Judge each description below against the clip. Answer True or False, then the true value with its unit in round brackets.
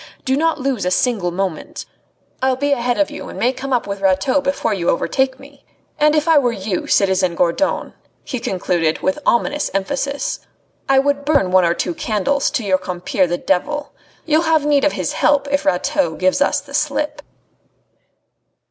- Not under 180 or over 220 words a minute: True (185 wpm)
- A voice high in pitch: True (260 Hz)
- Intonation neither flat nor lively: False (7.1 semitones)